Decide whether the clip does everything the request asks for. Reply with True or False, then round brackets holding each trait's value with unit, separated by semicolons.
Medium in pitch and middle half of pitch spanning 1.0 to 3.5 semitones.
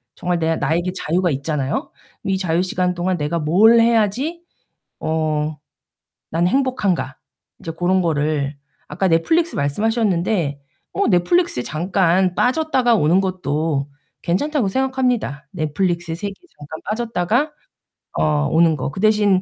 False (180 Hz; 5.6 semitones)